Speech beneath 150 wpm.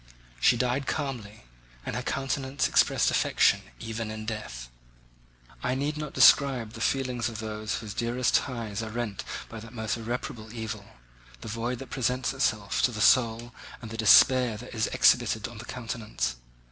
No: average, 165 wpm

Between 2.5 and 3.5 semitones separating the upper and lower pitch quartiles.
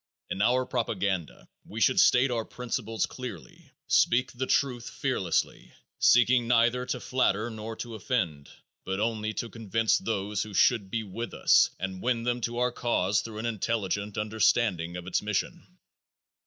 Yes: average, 3.1 semitones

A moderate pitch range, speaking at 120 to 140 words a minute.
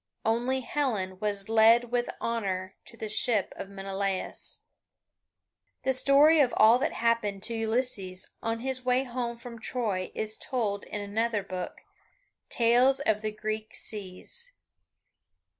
Yes: average, 3.5 semitones; slow, 135 wpm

